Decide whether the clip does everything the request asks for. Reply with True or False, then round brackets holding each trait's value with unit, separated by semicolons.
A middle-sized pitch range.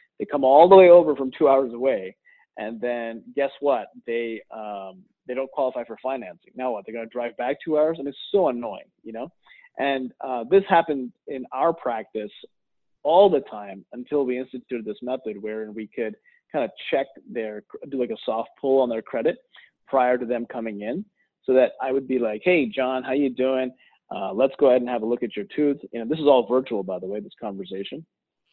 True (3.7 semitones)